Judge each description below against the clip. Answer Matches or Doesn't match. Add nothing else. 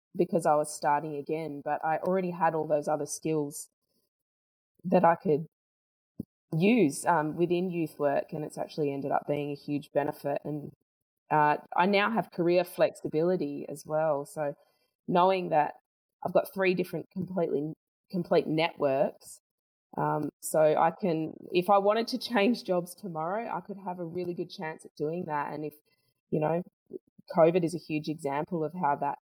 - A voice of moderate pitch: Matches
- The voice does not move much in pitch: Doesn't match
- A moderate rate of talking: Matches